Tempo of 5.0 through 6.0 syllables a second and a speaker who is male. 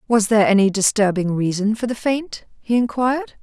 No: 5.5 syllables/s; female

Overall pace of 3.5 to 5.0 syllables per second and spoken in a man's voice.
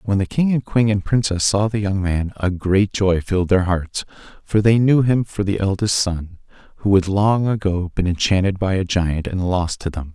Yes: 4.9 syllables/s; male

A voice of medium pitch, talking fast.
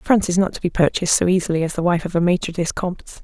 Yes: medium, 175 Hz; fast, 295 wpm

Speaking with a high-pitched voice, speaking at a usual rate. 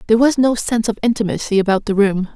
No: high, 220 Hz; fast, 230 wpm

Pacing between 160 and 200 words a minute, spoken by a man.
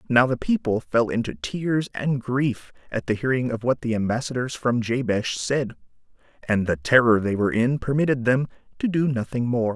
Yes: average, 185 wpm; male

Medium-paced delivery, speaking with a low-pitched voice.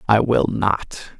Yes: average, 150 wpm; low, 105 Hz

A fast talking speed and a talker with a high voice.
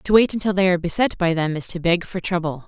No: fast, 290 wpm; medium, 175 Hz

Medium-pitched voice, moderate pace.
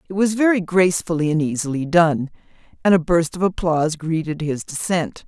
Yes: medium, 165 Hz; average, 170 wpm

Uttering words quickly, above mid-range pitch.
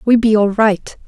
Yes: fast, 225 wpm; high, 215 Hz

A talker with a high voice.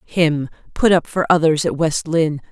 No: medium, 160 Hz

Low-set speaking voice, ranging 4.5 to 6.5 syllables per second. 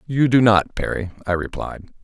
Yes: low, 110 Hz; 4.8 syllables/s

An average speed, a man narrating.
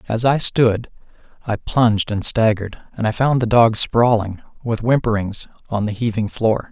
Yes: average, 170 wpm; male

